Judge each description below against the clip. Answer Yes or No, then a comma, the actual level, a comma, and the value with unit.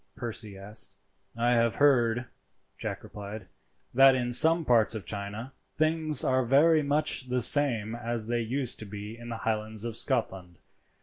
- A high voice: No, low, 120 Hz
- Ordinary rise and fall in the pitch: Yes, average, 3.6 semitones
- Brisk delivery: No, average, 160 wpm